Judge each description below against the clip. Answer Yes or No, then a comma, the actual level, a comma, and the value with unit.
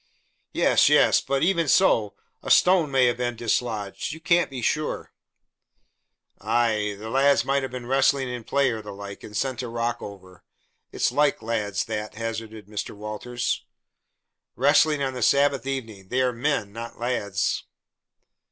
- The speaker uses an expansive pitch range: No, average, 4.1 semitones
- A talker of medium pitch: No, low, 120 Hz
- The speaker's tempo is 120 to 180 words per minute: Yes, average, 160 wpm